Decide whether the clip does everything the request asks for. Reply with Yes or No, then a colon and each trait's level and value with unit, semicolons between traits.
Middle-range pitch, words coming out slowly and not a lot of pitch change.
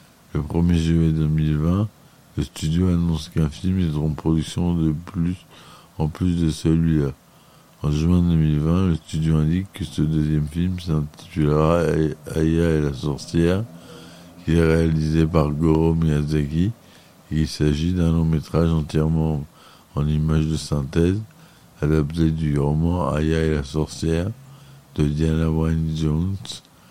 No: very low, 80 Hz; slow, 135 wpm; narrow, 1.8 semitones